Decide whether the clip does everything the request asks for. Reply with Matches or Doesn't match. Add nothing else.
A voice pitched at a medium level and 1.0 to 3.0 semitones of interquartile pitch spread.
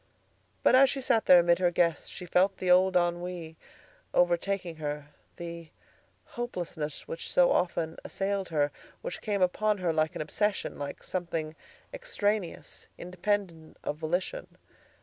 Doesn't match